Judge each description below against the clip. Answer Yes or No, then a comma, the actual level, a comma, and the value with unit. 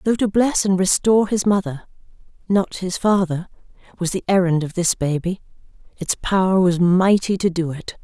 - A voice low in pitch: No, medium, 185 Hz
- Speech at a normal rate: Yes, average, 170 wpm